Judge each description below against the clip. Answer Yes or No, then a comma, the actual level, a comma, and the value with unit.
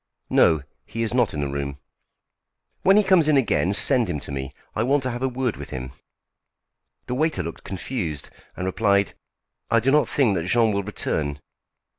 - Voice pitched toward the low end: Yes, low, 110 Hz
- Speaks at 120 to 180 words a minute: No, average, 190 wpm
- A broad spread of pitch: Yes, wide, 8.4 semitones